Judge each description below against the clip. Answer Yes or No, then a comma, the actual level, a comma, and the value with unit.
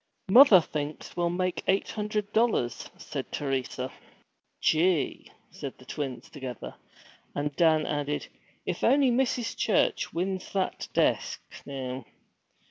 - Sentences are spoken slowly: Yes, slow, 120 wpm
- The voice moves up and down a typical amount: No, wide, 6.1 semitones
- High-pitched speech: No, medium, 165 Hz